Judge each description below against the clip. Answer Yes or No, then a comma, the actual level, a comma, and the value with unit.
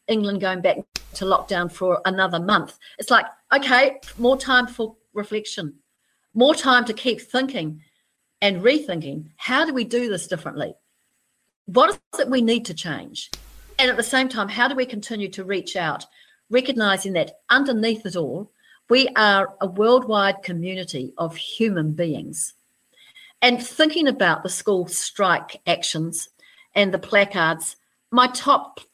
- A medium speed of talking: Yes, average, 150 wpm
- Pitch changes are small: No, wide, 5.5 semitones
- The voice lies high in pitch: Yes, high, 210 Hz